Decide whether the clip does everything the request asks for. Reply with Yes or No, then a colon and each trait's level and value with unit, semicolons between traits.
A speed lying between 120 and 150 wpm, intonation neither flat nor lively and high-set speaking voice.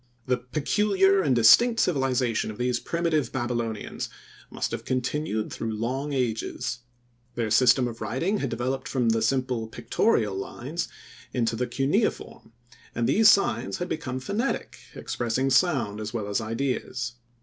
No: average, 140 wpm; average, 4.3 semitones; low, 125 Hz